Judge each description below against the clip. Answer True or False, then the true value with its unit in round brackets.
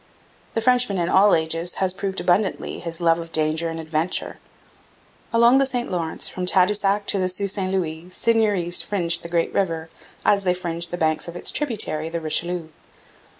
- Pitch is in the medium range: True (180 Hz)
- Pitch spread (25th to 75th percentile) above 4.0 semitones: False (3.2 semitones)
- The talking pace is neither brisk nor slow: True (180 wpm)